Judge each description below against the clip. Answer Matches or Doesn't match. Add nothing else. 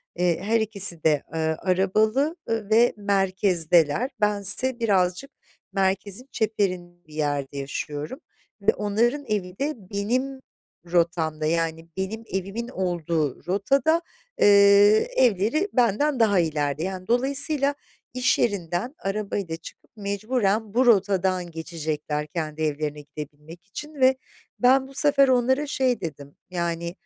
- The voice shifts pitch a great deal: Matches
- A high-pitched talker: Matches